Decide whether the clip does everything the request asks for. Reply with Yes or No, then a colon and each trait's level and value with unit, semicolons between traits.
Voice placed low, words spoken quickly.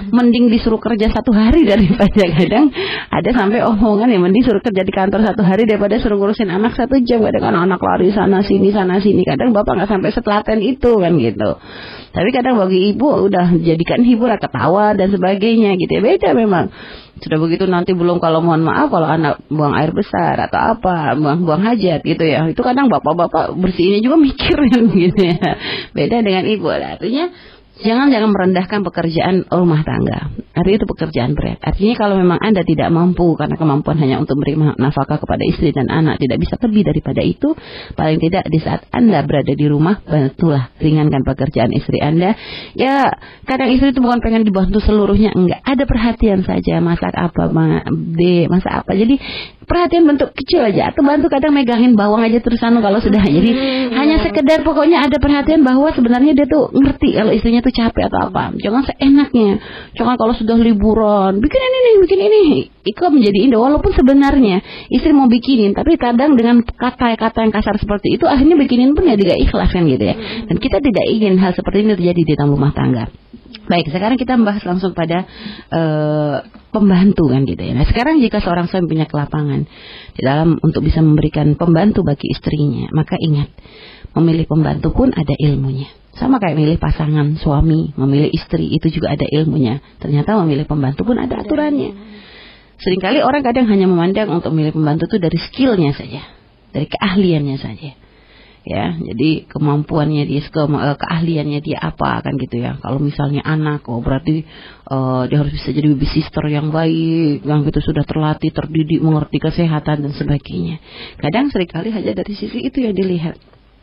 No: high, 190 Hz; fast, 175 wpm